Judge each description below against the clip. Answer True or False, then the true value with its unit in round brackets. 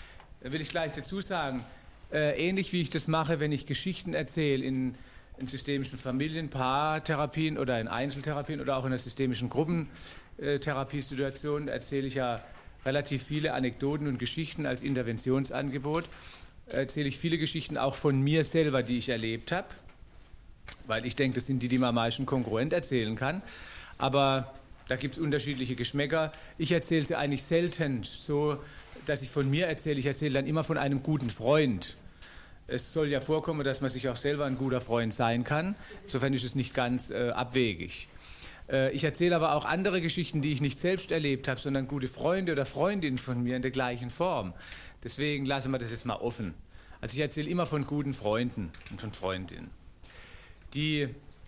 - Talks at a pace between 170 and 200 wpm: True (175 wpm)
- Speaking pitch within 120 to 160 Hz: True (135 Hz)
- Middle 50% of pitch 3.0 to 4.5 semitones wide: True (3.4 semitones)